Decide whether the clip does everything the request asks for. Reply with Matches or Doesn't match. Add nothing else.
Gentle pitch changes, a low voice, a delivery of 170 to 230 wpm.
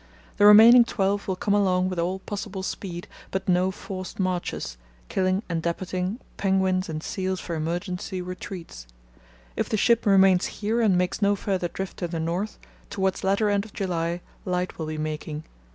Doesn't match